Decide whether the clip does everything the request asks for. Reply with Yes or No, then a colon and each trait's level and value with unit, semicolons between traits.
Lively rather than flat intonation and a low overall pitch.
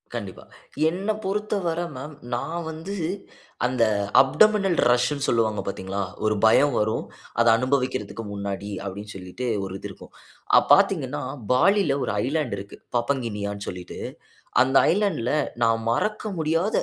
Yes: wide, 7.9 semitones; low, 130 Hz